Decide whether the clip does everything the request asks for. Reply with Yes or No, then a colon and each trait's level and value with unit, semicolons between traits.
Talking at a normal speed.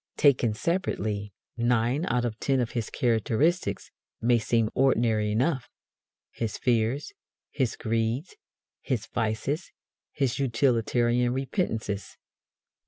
No: slow, 105 wpm